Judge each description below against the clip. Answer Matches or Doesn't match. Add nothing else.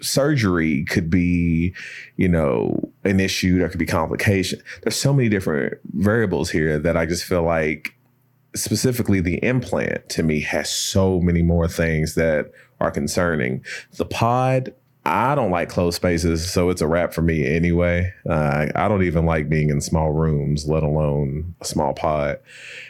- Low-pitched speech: Matches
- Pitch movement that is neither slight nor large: Matches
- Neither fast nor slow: Matches